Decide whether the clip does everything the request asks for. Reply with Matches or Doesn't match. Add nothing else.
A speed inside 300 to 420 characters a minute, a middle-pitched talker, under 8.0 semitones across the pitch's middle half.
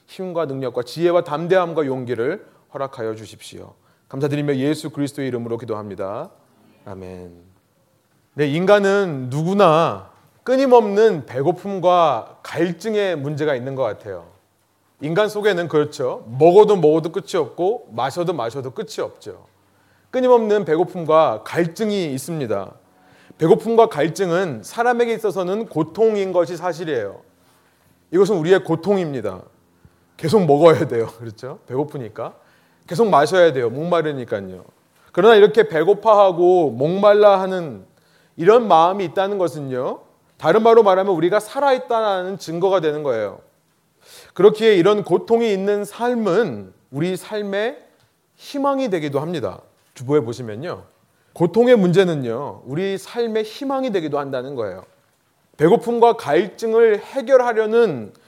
Matches